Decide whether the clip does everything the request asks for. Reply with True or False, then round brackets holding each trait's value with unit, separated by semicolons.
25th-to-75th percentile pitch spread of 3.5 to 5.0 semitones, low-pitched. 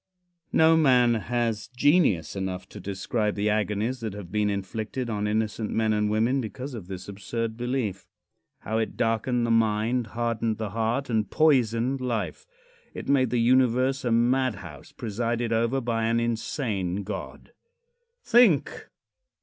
False (2.8 semitones; 115 Hz)